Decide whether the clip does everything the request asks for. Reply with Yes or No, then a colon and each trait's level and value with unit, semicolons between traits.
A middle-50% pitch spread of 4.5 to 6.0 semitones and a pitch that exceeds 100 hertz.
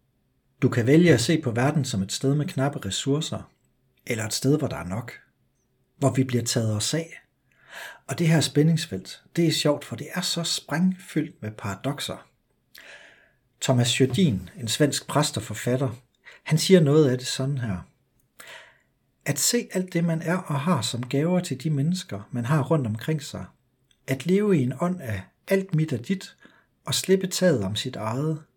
Yes: average, 4.9 semitones; medium, 140 Hz